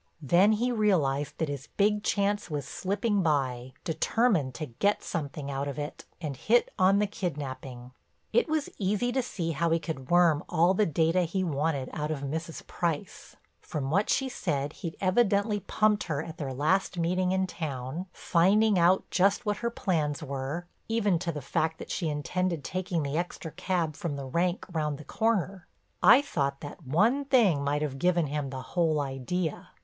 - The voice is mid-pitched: Yes, medium, 170 Hz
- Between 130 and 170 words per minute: No, average, 180 wpm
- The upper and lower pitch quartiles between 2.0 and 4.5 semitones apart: No, average, 5.2 semitones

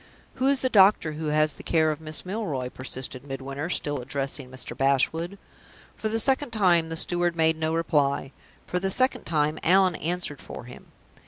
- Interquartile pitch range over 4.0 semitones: Yes, average, 4.4 semitones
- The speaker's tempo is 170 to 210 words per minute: Yes, average, 180 wpm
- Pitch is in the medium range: Yes, medium, 160 Hz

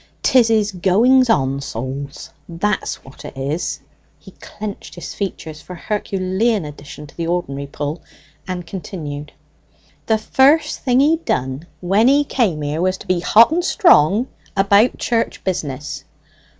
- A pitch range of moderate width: No, wide, 7.2 semitones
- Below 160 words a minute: Yes, average, 150 wpm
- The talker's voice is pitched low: No, medium, 185 Hz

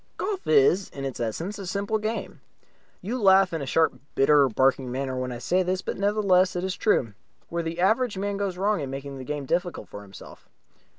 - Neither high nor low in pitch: Yes, medium, 180 Hz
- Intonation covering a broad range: Yes, wide, 6.7 semitones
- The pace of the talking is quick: Yes, fast, 215 wpm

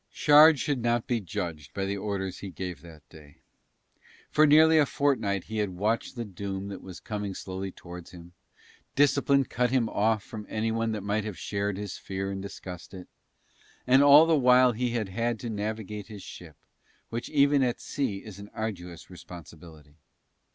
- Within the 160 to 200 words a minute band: Yes, average, 180 wpm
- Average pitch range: Yes, average, 4.5 semitones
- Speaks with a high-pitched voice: No, low, 105 Hz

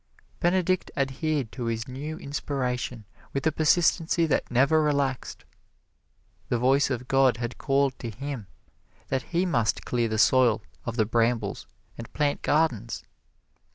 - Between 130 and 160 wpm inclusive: Yes, average, 140 wpm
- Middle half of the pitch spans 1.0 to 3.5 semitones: No, average, 4.1 semitones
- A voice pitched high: No, low, 135 Hz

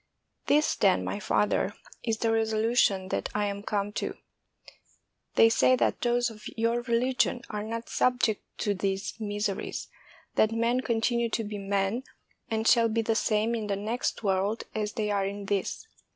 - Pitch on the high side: Yes, high, 220 Hz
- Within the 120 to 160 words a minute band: No, average, 175 wpm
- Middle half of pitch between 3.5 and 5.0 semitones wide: No, narrow, 2.4 semitones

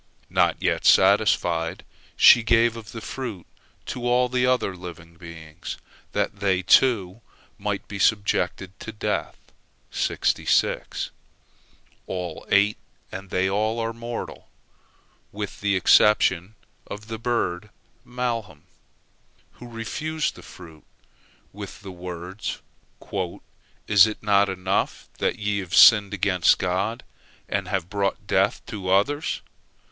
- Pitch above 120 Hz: No, low, 100 Hz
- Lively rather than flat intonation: No, average, 3.6 semitones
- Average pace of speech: No, slow, 115 wpm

